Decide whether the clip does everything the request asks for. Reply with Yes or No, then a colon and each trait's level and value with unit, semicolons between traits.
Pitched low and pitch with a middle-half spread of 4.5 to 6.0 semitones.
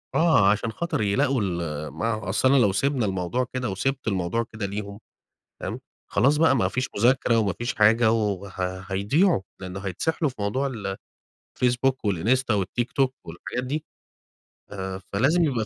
Yes: low, 115 Hz; average, 4.9 semitones